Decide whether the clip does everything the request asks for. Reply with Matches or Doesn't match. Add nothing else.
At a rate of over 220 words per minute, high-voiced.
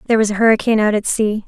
Matches